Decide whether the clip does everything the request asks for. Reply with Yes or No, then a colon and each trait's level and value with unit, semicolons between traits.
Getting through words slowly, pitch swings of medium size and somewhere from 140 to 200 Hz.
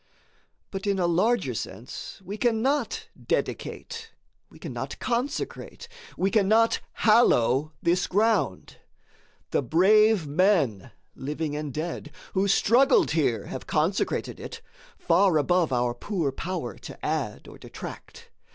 No: slow, 115 wpm; wide, 6.8 semitones; medium, 185 Hz